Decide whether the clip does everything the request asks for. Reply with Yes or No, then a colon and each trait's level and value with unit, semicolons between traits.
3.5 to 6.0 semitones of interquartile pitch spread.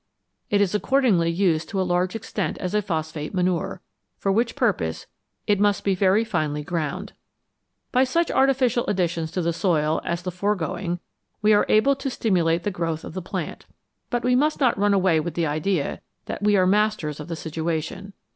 Yes: average, 4.0 semitones